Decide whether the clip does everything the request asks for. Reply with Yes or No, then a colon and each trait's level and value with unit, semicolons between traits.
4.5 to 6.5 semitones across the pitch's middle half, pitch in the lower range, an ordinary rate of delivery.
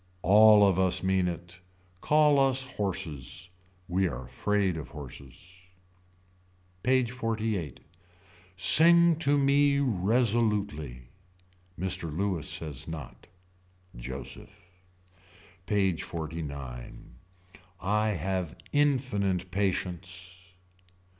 No: average, 5.1 semitones; very low, 95 Hz; slow, 85 wpm